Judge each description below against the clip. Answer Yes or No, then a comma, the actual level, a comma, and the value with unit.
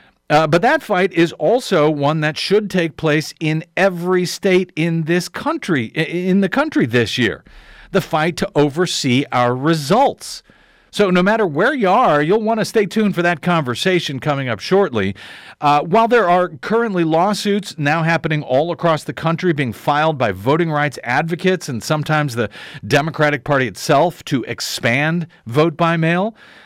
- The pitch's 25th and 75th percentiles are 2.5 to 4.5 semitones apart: Yes, average, 4.0 semitones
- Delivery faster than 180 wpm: No, average, 165 wpm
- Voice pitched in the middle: Yes, medium, 165 Hz